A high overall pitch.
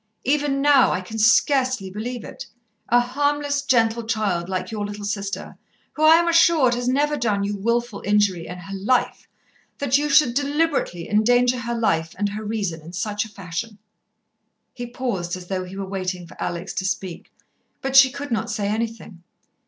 Yes: high, 225 Hz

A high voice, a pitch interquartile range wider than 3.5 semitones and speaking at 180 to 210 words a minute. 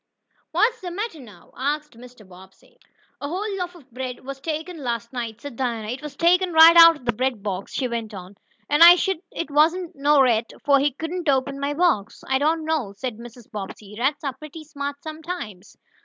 Yes: very high, 280 Hz; wide, 5.5 semitones; average, 200 wpm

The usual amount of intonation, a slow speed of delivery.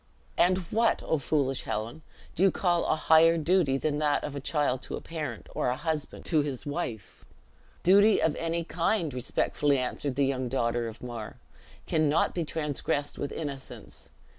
No: average, 4.0 semitones; average, 175 wpm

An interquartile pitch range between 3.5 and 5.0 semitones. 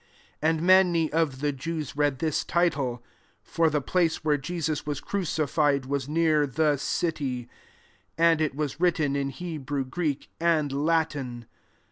No: average, 2.8 semitones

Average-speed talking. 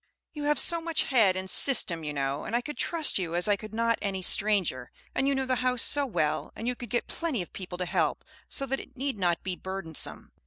No: fast, 245 wpm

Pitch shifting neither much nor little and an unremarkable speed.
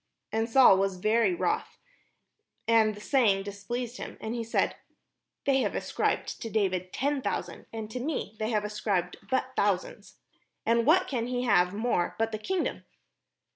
Yes: average, 3.5 semitones; average, 165 wpm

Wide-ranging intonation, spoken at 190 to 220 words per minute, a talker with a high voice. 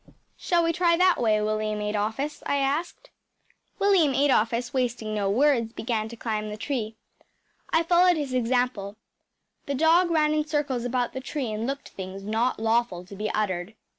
No: wide, 5.7 semitones; average, 165 wpm; high, 245 Hz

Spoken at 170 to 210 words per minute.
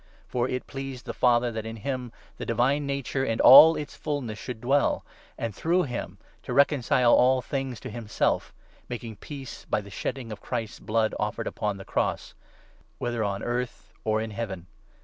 Yes: average, 190 wpm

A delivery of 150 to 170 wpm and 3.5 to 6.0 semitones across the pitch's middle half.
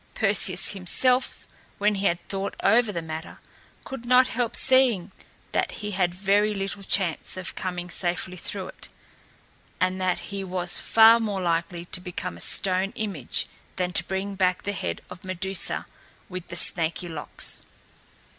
No: average, 155 wpm; narrow, 2.4 semitones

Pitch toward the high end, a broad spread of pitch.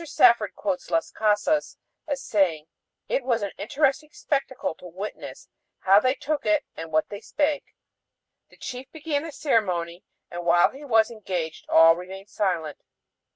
Yes: high, 215 Hz; wide, 7.9 semitones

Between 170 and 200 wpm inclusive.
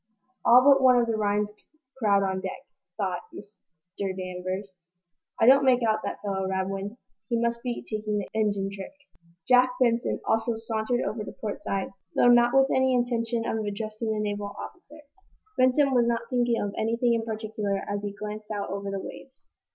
Yes: average, 180 wpm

